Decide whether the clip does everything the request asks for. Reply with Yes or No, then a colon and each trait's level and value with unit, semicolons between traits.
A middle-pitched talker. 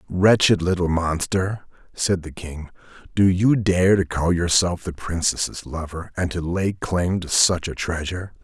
No: very low, 90 Hz